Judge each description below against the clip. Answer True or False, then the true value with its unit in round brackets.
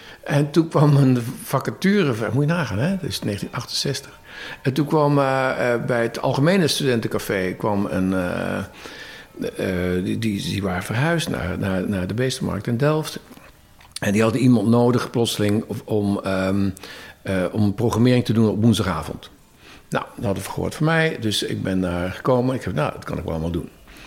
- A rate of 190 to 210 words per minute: False (180 wpm)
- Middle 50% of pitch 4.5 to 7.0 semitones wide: True (5.3 semitones)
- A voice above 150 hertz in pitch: False (115 Hz)